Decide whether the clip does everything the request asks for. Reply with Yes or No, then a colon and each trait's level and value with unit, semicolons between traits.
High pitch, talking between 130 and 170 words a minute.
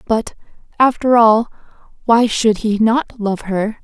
Yes: high, 225 Hz; average, 140 wpm